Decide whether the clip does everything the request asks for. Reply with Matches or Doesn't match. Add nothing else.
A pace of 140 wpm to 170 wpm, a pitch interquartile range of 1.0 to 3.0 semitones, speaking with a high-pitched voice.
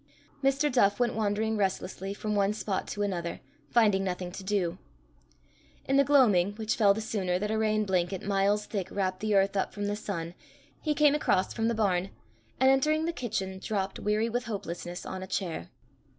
Doesn't match